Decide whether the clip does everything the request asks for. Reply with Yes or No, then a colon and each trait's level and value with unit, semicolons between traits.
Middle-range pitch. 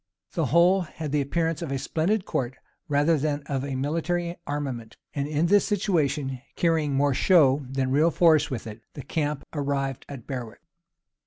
Yes: medium, 145 Hz